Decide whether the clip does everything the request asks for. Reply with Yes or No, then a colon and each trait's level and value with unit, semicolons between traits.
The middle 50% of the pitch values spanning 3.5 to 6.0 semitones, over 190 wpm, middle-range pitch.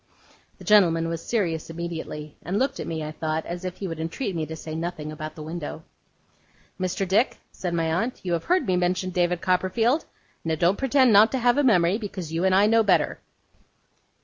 Yes: average, 4.0 semitones; fast, 205 wpm; medium, 180 Hz